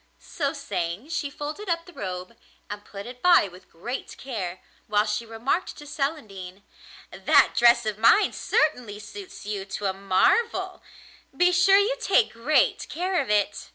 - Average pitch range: No, wide, 8.4 semitones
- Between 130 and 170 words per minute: Yes, average, 160 wpm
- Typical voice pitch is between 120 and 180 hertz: No, high, 240 Hz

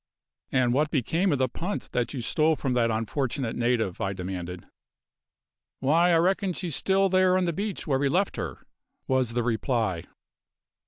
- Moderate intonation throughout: No, wide, 6.9 semitones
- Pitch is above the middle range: No, low, 135 Hz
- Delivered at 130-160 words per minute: No, average, 170 wpm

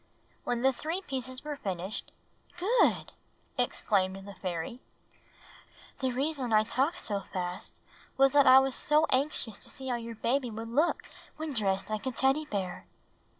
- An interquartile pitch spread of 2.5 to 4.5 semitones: No, average, 5.2 semitones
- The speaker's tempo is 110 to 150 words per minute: No, average, 160 wpm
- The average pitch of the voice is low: No, very high, 250 Hz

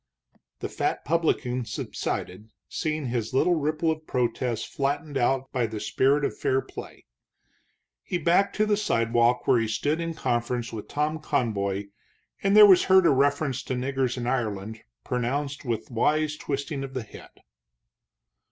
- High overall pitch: No, low, 135 Hz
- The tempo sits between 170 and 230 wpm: No, average, 155 wpm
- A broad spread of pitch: No, average, 4.5 semitones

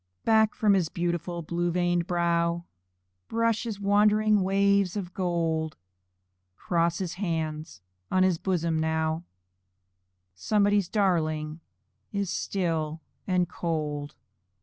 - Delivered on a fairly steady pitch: No, average, 3.6 semitones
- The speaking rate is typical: No, slow, 105 wpm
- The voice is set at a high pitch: No, medium, 175 Hz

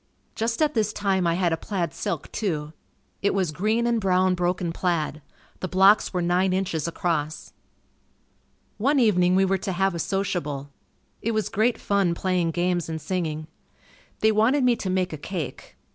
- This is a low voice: No, medium, 185 Hz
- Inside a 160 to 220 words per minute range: Yes, average, 175 wpm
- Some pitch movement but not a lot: Yes, average, 3.2 semitones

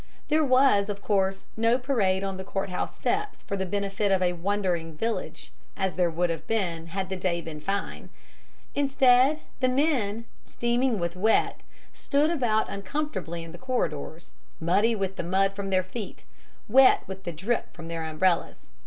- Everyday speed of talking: Yes, average, 170 wpm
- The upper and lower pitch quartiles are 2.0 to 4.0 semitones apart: No, average, 5.0 semitones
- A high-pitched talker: Yes, high, 195 Hz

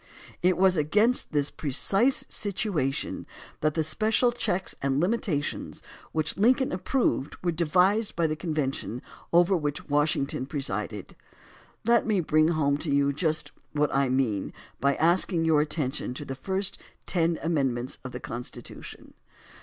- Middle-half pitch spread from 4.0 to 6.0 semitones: Yes, average, 4.8 semitones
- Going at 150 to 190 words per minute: No, average, 140 wpm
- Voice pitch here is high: No, medium, 155 Hz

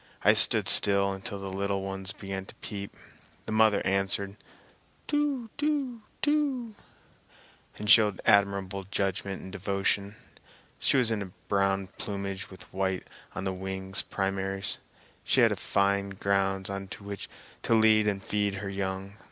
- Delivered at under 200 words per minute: Yes, average, 140 wpm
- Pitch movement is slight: Yes, narrow, 1.3 semitones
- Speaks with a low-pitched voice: Yes, low, 100 Hz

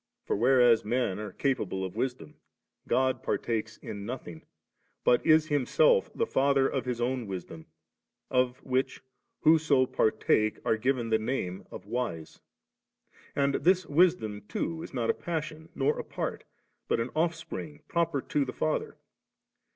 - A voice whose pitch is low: Yes, low, 130 Hz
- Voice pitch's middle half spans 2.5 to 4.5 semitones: No, average, 5.3 semitones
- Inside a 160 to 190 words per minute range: No, average, 150 wpm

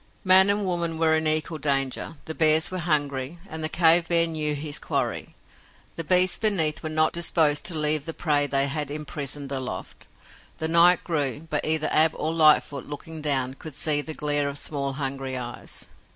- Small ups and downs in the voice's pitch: Yes, narrow, 2.2 semitones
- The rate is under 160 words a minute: No, average, 185 wpm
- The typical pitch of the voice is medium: Yes, medium, 155 Hz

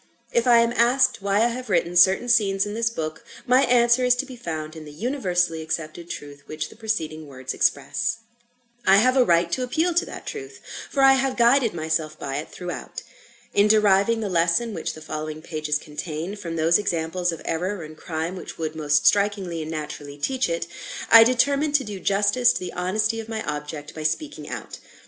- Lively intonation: Yes, wide, 6.9 semitones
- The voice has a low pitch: No, high, 190 Hz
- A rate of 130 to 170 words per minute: No, average, 200 wpm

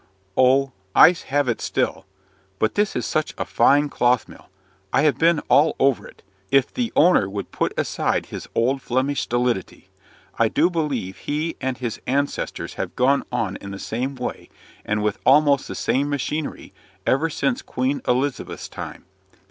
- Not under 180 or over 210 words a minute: No, average, 165 wpm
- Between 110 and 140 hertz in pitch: Yes, low, 135 Hz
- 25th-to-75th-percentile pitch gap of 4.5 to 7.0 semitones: No, average, 3.4 semitones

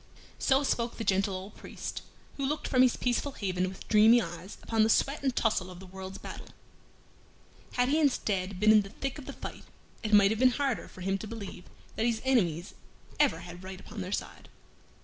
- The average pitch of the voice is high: Yes, high, 215 Hz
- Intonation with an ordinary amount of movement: Yes, average, 4.8 semitones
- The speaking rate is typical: No, fast, 210 wpm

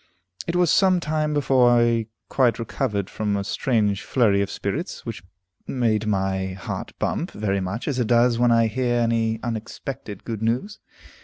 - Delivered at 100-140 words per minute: No, average, 165 wpm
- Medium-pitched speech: No, low, 115 Hz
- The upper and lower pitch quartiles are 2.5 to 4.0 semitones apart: Yes, average, 3.6 semitones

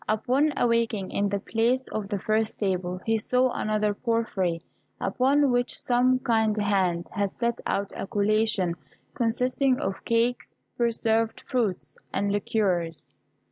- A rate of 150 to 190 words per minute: No, average, 140 wpm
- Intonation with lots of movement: No, average, 3.3 semitones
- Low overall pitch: No, high, 220 Hz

